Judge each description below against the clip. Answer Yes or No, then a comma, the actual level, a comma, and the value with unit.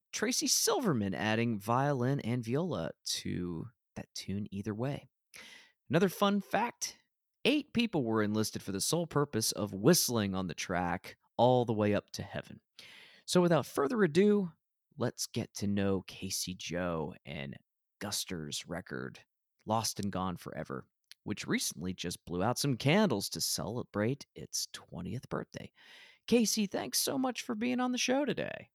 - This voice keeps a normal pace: Yes, average, 150 wpm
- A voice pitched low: Yes, low, 120 Hz